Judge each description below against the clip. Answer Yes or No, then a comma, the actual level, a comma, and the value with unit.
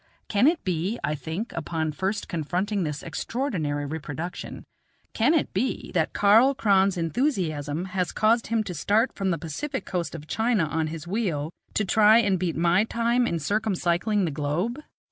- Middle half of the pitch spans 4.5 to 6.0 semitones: Yes, wide, 5.5 semitones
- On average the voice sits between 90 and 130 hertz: No, medium, 185 Hz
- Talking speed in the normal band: Yes, average, 165 wpm